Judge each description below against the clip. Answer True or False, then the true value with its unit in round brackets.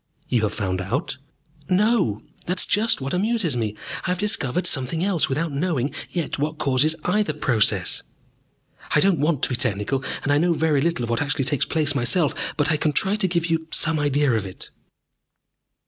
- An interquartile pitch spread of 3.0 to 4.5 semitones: False (4.9 semitones)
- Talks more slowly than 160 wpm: False (195 wpm)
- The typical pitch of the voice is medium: True (150 Hz)